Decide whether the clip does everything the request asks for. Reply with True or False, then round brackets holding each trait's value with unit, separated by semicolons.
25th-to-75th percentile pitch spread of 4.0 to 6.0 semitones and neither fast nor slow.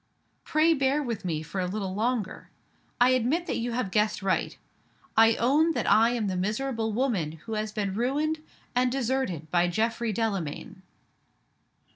True (4.7 semitones; 160 wpm)